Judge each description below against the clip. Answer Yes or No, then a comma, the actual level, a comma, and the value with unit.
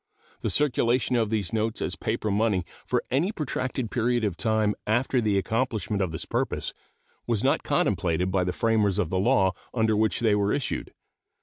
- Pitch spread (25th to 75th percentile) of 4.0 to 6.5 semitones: No, average, 3.4 semitones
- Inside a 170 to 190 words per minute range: Yes, average, 180 wpm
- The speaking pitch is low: Yes, low, 110 Hz